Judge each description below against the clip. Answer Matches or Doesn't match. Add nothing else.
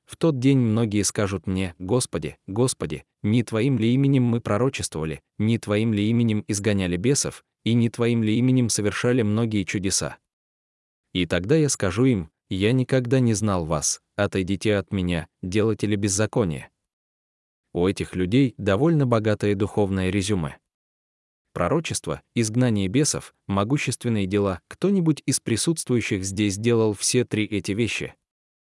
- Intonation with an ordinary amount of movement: Matches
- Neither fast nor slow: Matches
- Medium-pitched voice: Doesn't match